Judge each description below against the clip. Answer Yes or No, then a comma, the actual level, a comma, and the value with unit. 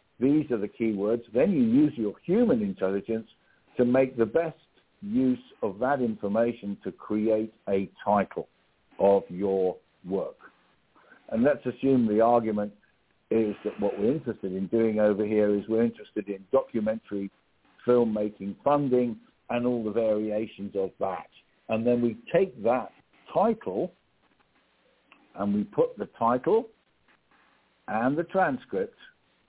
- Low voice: Yes, low, 115 Hz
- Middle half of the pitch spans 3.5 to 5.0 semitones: Yes, average, 4.2 semitones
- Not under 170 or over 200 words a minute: No, slow, 135 wpm